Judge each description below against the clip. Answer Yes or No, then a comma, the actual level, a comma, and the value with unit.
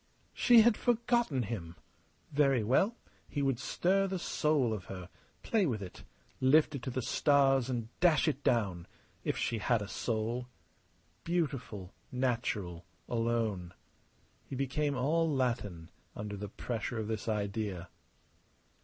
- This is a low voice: Yes, low, 125 Hz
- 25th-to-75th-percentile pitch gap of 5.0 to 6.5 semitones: Yes, wide, 5.6 semitones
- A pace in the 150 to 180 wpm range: No, slow, 135 wpm